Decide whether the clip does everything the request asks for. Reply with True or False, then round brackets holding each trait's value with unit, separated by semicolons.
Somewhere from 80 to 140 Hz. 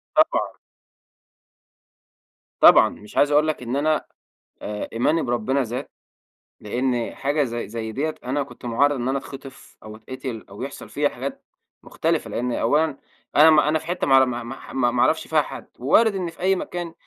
True (135 Hz)